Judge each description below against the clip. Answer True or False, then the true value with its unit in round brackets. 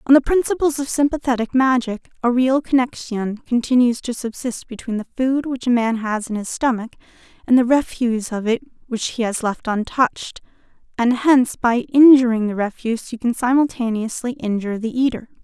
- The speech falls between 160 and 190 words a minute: True (170 wpm)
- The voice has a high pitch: True (245 Hz)